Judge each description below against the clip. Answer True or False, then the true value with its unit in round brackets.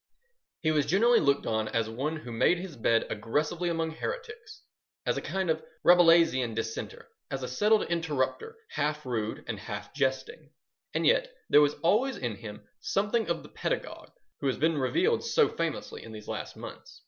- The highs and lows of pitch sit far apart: True (7.5 semitones)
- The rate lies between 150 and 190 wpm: True (175 wpm)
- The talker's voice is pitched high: False (155 Hz)